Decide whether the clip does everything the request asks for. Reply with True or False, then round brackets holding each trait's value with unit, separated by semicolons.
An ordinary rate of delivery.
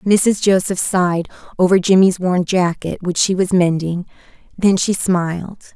True (145 wpm)